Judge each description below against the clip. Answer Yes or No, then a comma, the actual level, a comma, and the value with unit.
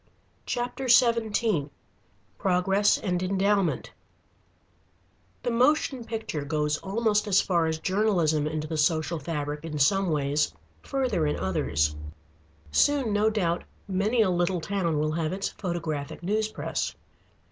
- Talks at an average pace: No, slow, 125 wpm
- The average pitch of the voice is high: No, medium, 180 Hz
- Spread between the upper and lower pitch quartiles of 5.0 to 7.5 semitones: Yes, wide, 5.6 semitones